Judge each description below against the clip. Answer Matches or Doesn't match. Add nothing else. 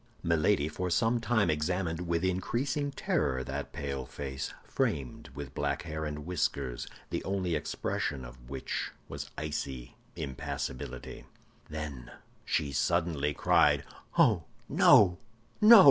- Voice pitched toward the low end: Matches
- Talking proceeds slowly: Matches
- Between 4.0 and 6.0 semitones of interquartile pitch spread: Matches